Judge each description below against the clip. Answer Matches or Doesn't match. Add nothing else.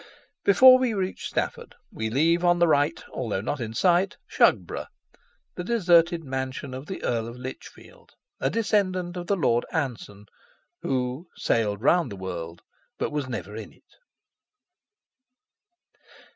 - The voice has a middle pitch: Matches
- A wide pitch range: Matches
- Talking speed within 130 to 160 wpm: Matches